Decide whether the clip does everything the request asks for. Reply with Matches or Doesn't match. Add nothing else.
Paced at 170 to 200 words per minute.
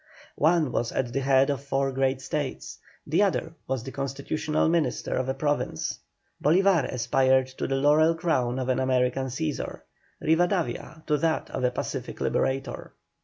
Doesn't match